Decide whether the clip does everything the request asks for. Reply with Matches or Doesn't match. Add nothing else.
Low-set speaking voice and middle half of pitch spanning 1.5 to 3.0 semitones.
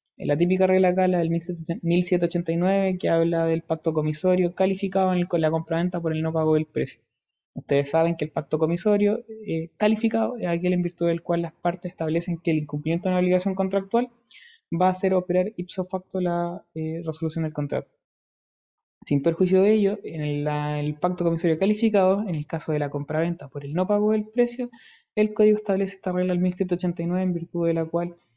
Doesn't match